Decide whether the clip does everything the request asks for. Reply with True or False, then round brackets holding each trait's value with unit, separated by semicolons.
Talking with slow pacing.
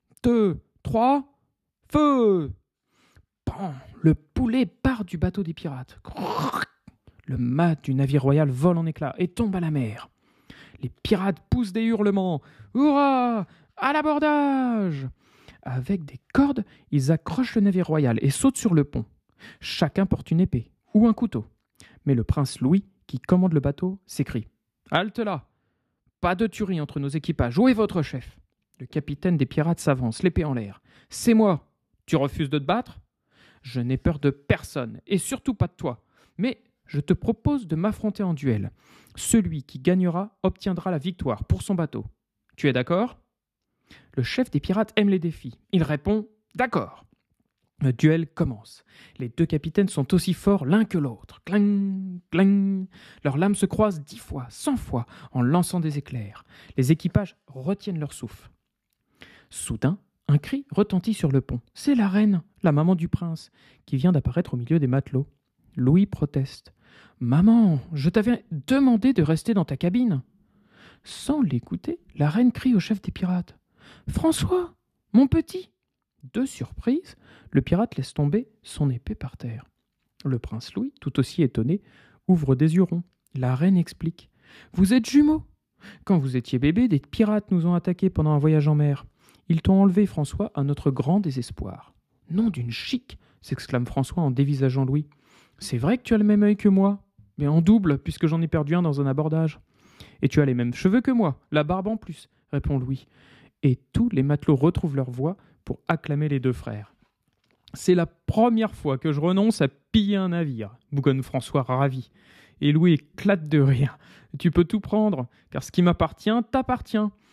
False (170 wpm)